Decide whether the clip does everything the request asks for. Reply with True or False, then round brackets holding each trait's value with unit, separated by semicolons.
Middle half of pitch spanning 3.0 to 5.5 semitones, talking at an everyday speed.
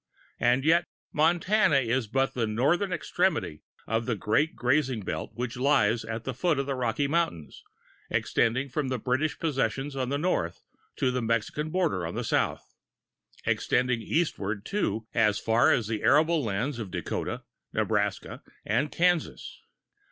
True (5.1 semitones; 150 wpm)